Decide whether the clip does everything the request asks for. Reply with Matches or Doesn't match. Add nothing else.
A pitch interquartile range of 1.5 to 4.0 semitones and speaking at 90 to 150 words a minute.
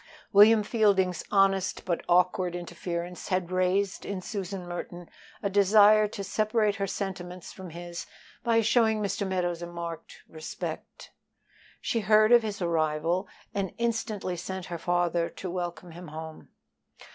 Matches